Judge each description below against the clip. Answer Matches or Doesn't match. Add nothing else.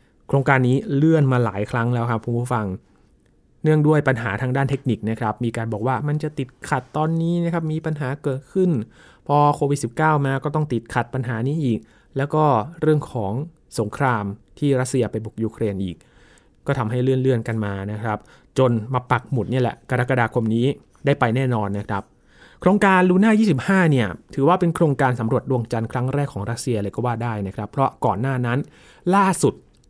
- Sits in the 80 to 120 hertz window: Doesn't match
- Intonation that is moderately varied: Matches